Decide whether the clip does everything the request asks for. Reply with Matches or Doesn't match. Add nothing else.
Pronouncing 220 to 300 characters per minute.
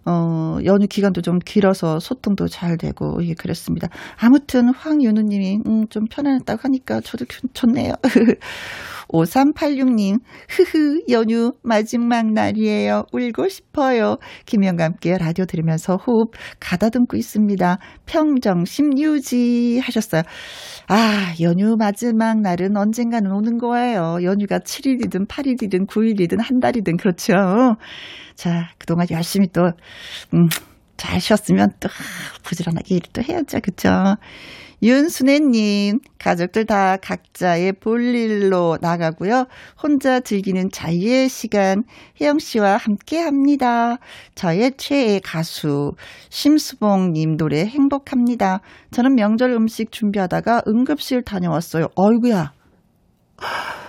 Matches